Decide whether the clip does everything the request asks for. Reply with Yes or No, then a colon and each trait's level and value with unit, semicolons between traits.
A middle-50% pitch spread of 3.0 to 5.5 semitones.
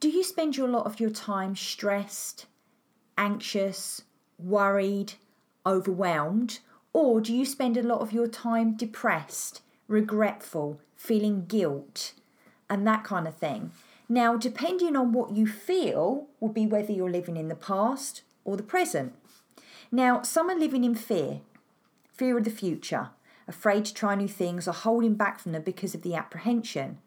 Yes: average, 3.5 semitones